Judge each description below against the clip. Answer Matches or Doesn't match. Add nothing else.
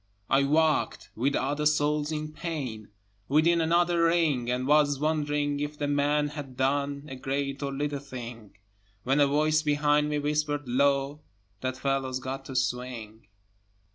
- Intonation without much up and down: Matches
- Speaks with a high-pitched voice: Doesn't match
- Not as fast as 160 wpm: Matches